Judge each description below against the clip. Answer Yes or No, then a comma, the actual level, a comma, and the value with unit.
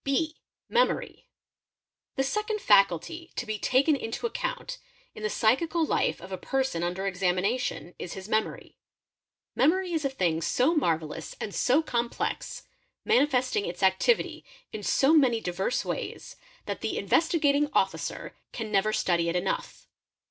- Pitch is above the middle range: Yes, high, 245 Hz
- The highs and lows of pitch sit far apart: Yes, wide, 8.6 semitones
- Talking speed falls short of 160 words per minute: Yes, average, 145 wpm